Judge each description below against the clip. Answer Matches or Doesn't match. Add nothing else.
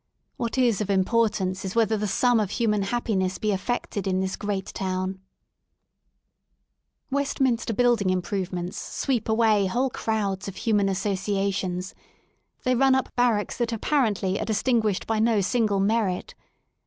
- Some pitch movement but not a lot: Matches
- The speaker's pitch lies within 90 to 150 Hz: Doesn't match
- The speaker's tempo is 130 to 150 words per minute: Matches